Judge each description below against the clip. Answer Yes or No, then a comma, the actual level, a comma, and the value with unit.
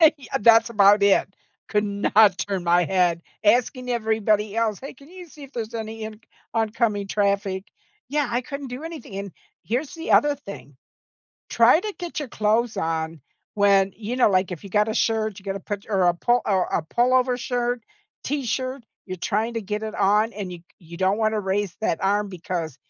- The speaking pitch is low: No, high, 215 Hz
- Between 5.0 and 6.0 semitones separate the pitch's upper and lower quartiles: No, average, 3.8 semitones